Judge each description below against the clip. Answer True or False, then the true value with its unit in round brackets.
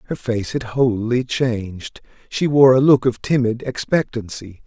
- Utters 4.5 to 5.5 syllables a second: False (4.3 syllables/s)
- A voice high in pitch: False (120 Hz)